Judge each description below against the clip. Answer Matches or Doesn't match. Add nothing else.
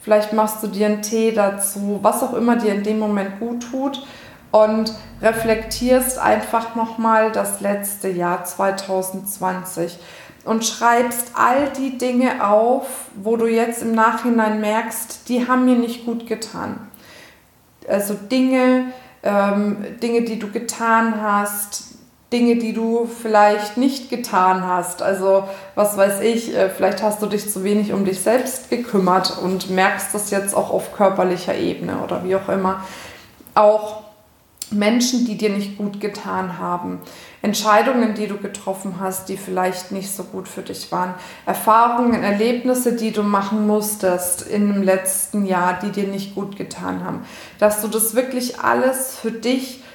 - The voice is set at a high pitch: Matches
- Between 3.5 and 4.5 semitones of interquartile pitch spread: Doesn't match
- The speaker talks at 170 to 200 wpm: Doesn't match